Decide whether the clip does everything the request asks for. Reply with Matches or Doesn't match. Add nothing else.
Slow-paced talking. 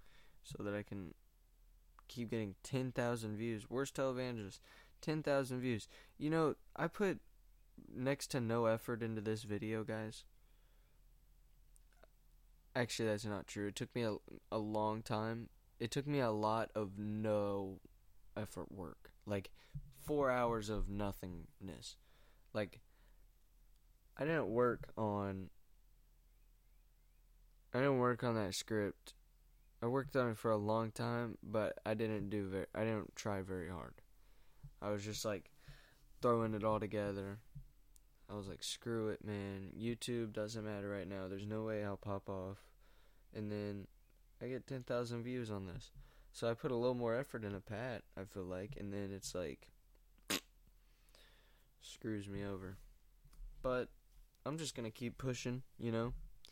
Doesn't match